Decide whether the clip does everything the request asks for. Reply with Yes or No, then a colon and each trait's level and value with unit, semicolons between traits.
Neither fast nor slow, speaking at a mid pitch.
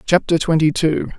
Yes: average, 150 wpm; medium, 160 Hz